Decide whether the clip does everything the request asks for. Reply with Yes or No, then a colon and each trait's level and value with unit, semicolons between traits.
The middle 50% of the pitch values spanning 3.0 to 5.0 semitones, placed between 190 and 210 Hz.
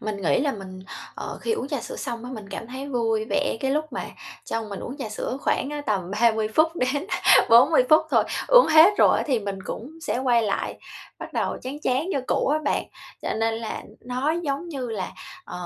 No: average, 4.7 semitones; very high, 250 Hz